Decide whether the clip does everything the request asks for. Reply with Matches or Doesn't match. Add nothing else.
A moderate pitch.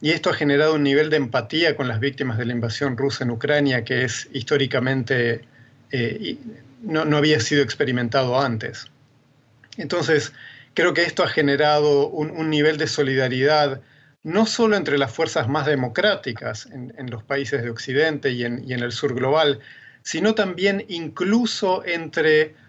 Matches